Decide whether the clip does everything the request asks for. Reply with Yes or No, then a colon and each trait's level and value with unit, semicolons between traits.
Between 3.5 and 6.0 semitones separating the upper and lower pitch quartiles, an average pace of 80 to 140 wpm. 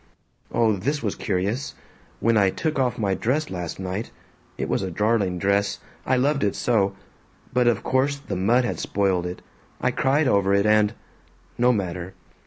No: average, 4.5 semitones; average, 175 wpm